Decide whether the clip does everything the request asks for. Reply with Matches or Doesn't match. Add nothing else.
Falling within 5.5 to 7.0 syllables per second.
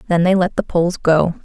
Matches